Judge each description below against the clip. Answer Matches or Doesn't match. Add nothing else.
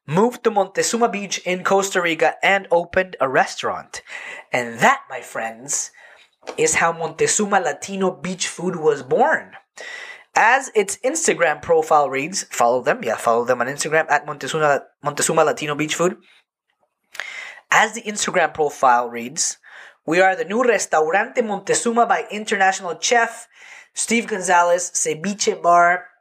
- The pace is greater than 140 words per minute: Doesn't match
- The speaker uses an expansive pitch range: Matches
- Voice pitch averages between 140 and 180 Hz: Doesn't match